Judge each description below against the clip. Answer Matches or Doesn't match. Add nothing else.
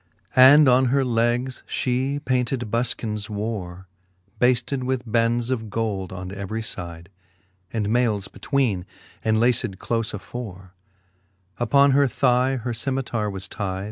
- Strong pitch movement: Doesn't match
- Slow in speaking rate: Matches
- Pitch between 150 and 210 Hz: Doesn't match